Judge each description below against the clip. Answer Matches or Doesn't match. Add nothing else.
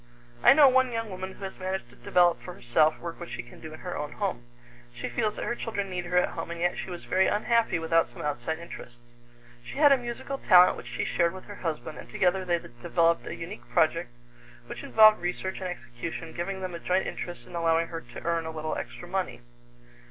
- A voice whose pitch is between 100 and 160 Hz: Doesn't match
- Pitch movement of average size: Matches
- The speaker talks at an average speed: Doesn't match